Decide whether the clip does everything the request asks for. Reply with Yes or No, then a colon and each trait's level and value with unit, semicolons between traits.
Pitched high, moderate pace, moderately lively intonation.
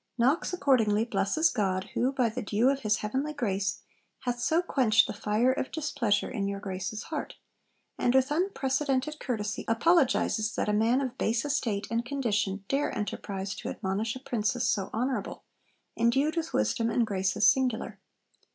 Yes: high, 235 Hz; average, 160 wpm; average, 4.5 semitones